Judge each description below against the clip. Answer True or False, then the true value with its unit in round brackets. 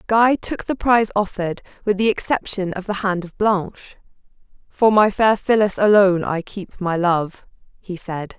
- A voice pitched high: True (200 Hz)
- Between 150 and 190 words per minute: True (170 wpm)